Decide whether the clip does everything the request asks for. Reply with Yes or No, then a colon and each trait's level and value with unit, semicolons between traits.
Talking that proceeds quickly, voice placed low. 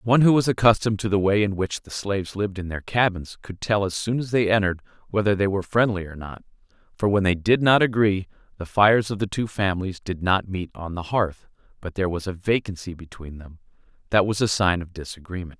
Yes: fast, 225 wpm; low, 100 Hz